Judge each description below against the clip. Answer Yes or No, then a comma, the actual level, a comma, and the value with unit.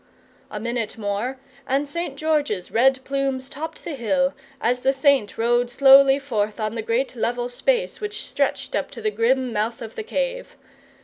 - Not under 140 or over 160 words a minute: No, average, 175 wpm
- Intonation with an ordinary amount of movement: Yes, average, 3.5 semitones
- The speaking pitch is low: No, very high, 260 Hz